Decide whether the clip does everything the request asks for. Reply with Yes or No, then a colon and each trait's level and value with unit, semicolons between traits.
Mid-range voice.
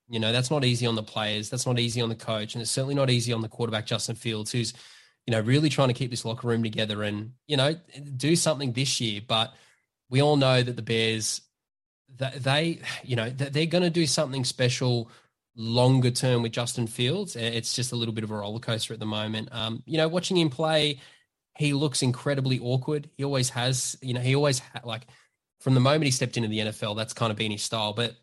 No: low, 125 Hz